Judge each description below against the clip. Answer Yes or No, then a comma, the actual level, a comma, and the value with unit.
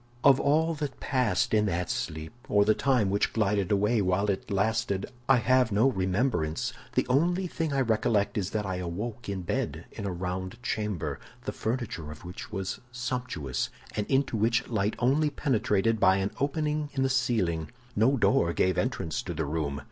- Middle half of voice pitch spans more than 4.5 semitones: Yes, wide, 5.5 semitones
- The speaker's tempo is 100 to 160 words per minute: No, average, 180 wpm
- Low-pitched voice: Yes, low, 105 Hz